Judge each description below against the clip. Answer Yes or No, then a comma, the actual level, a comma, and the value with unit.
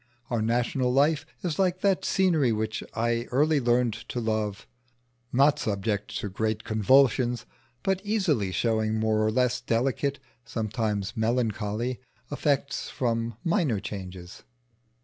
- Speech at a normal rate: No, slow, 125 wpm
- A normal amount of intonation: Yes, average, 4.2 semitones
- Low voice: Yes, low, 120 Hz